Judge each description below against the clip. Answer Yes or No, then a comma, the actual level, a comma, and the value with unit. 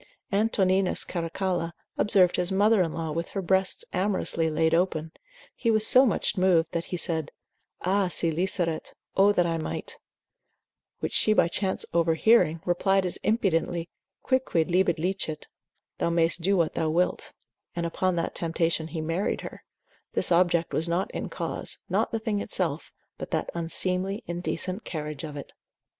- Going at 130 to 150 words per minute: No, average, 160 wpm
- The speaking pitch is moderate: Yes, medium, 175 Hz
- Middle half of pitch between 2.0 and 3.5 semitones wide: Yes, average, 2.7 semitones